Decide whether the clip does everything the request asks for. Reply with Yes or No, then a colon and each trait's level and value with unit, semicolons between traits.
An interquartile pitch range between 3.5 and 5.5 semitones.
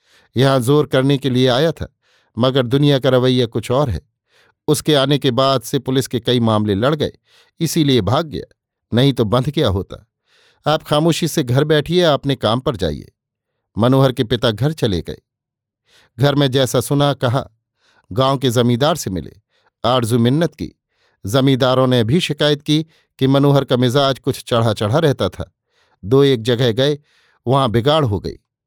No: average, 3.0 semitones